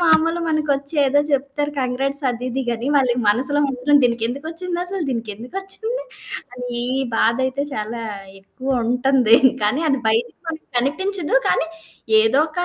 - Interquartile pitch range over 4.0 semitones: Yes, average, 4.6 semitones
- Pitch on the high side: Yes, very high, 275 Hz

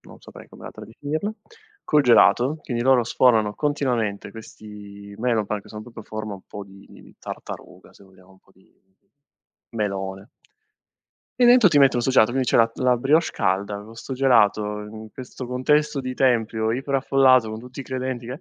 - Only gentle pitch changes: No, average, 3.9 semitones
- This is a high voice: No, low, 115 Hz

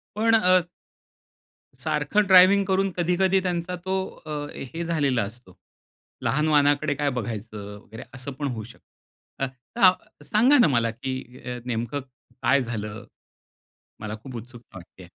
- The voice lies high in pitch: No, medium, 140 Hz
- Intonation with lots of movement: Yes, wide, 7.6 semitones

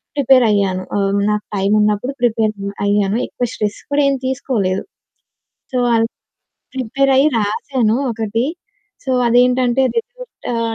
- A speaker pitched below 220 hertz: No, high, 225 Hz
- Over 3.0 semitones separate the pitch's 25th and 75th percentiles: Yes, average, 4.1 semitones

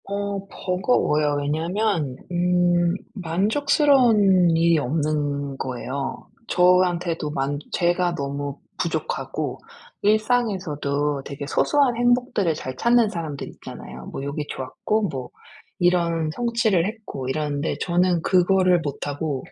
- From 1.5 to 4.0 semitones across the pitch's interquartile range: No, wide, 5.6 semitones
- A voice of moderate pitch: Yes, medium, 175 Hz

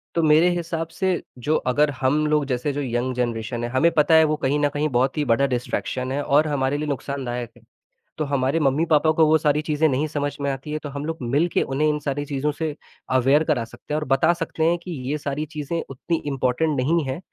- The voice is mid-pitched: Yes, medium, 145 Hz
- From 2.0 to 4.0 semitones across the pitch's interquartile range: Yes, average, 2.7 semitones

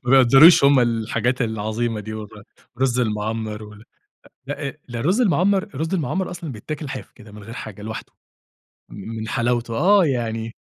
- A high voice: No, low, 120 Hz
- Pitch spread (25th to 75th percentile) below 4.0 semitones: No, average, 4.7 semitones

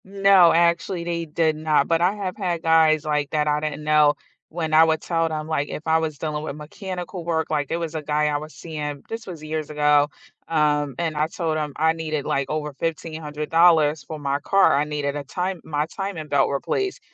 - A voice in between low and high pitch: Yes, medium, 155 Hz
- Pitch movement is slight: Yes, narrow, 1.9 semitones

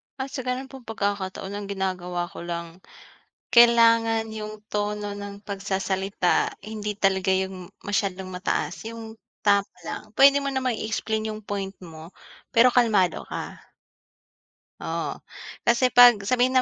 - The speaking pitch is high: Yes, high, 205 Hz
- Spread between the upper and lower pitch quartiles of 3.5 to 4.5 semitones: No, average, 3.1 semitones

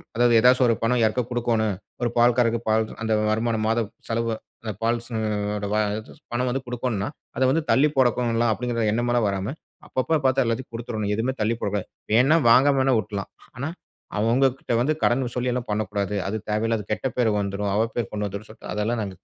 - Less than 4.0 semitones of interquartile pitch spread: Yes, narrow, 2.5 semitones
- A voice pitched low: Yes, low, 115 Hz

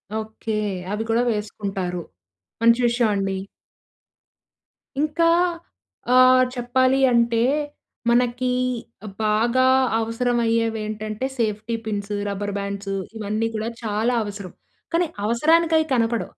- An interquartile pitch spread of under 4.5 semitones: Yes, narrow, 2.6 semitones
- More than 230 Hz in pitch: No, high, 225 Hz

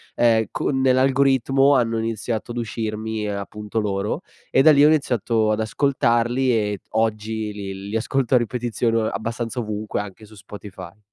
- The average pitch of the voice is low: Yes, low, 110 Hz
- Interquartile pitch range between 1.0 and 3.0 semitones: Yes, average, 2.7 semitones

